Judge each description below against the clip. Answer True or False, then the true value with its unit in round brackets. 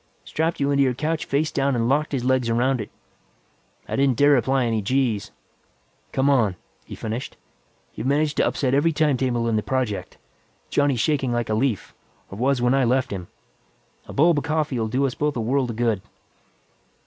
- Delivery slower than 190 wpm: False (195 wpm)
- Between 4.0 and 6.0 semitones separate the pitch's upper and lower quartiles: False (3.2 semitones)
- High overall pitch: False (130 Hz)